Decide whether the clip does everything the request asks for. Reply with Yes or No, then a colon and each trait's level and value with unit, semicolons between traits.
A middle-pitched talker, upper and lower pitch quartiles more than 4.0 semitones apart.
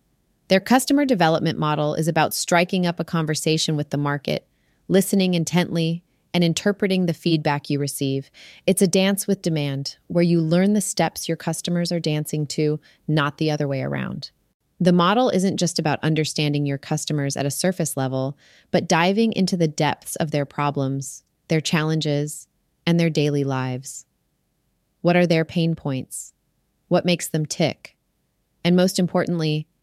No: medium, 160 Hz; average, 3.2 semitones